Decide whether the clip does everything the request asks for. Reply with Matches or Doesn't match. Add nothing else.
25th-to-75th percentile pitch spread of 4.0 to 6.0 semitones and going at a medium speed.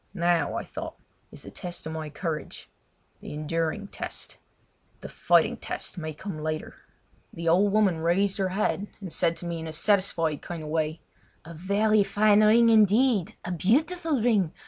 Matches